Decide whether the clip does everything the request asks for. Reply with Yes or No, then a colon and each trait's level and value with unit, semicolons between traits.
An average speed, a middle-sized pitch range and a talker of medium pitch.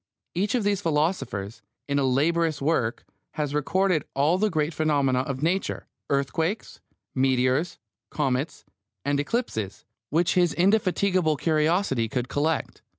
No: slow, 125 wpm; average, 4.5 semitones; medium, 155 Hz